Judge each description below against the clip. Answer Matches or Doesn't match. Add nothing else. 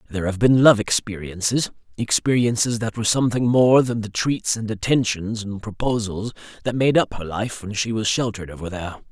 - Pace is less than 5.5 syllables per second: Doesn't match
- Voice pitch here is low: Matches